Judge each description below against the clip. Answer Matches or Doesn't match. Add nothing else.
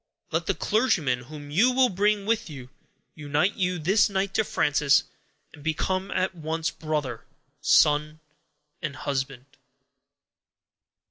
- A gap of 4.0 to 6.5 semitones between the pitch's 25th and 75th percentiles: Matches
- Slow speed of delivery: Matches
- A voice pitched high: Doesn't match